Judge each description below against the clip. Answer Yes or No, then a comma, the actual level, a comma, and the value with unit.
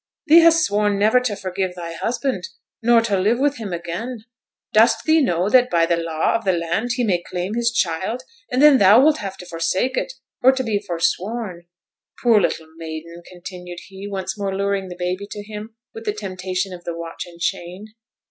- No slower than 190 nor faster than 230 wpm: Yes, average, 200 wpm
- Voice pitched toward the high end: Yes, high, 200 Hz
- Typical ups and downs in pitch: Yes, average, 4.6 semitones